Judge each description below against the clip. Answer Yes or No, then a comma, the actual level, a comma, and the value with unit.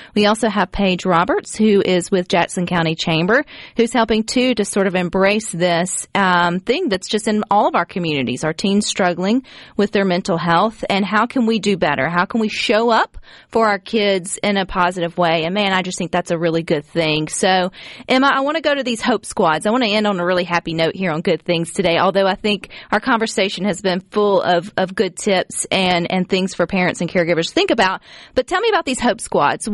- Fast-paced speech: Yes, fast, 235 wpm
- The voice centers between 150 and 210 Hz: Yes, high, 190 Hz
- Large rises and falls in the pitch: No, average, 3.5 semitones